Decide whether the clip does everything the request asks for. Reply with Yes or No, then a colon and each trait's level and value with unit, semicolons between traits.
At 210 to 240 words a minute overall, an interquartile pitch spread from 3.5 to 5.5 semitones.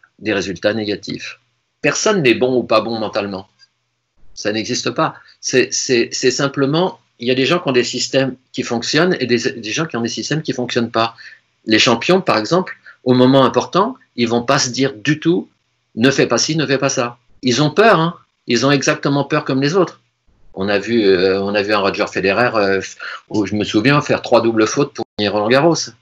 Yes: fast, 220 wpm; average, 4.7 semitones